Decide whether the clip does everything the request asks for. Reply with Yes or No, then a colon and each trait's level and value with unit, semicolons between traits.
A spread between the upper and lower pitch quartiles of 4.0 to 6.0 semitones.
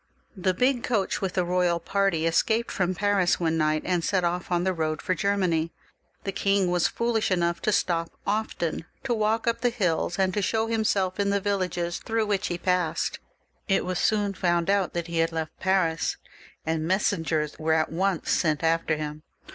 No: average, 3.3 semitones